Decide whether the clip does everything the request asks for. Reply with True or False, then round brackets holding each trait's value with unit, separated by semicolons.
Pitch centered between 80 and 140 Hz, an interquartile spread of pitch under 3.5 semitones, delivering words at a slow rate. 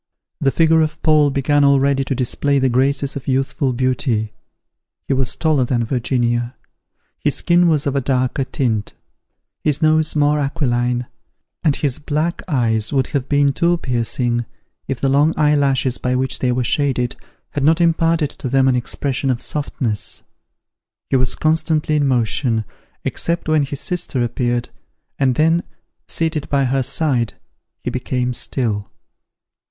False (135 Hz; 3.1 semitones; 155 wpm)